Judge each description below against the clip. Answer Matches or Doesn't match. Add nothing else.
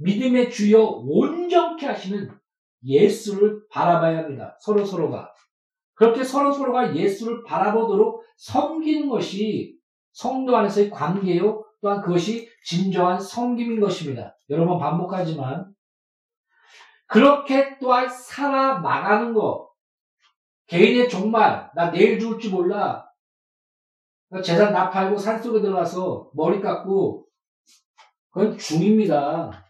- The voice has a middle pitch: Doesn't match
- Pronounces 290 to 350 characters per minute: Doesn't match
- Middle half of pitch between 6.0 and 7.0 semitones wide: Doesn't match